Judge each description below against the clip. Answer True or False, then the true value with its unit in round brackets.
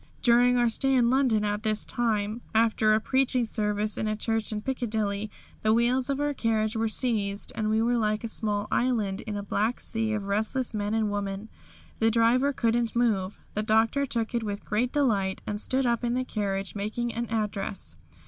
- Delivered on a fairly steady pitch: True (2.3 semitones)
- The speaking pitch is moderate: False (220 Hz)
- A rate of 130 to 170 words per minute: False (195 wpm)